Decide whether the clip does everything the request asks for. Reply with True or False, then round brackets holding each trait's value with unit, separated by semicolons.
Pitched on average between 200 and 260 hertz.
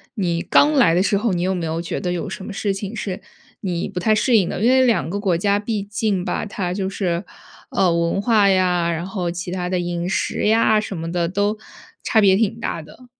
False (190 Hz)